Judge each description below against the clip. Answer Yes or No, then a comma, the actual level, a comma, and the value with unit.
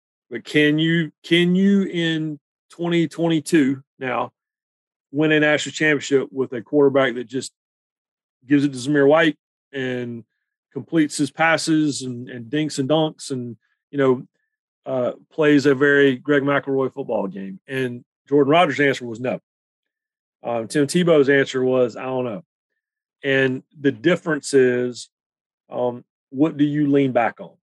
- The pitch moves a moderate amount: Yes, average, 3.2 semitones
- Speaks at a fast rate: No, average, 145 wpm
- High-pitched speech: No, medium, 140 Hz